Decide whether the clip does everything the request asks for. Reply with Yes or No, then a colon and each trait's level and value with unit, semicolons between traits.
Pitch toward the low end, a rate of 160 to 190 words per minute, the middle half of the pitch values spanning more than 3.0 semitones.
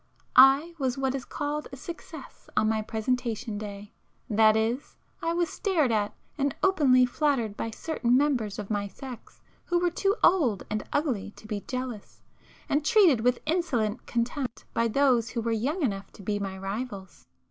No: high, 245 Hz; average, 180 wpm; average, 5.1 semitones